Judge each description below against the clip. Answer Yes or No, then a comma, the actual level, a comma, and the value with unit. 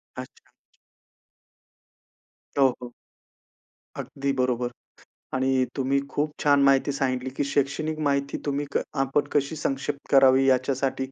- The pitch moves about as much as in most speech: No, narrow, 1.3 semitones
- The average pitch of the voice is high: No, low, 135 Hz